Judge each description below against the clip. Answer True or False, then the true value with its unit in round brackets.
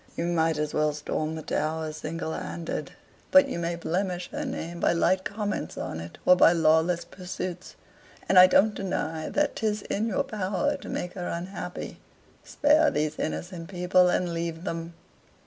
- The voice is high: False (175 Hz)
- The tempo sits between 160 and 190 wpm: True (170 wpm)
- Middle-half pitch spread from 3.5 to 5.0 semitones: False (3.0 semitones)